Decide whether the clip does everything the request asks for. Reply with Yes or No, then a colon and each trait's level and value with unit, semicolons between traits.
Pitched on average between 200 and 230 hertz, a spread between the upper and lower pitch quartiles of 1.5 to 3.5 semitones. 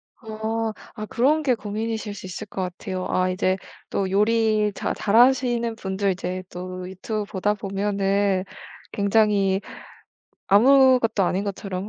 Yes: high, 205 Hz; average, 2.7 semitones